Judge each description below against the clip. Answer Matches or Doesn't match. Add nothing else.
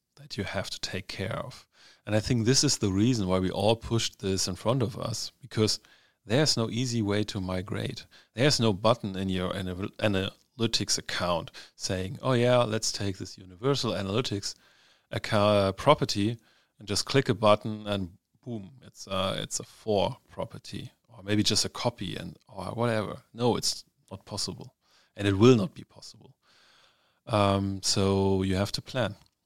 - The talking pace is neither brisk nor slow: Matches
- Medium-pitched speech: Doesn't match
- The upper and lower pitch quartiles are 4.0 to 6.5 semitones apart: Doesn't match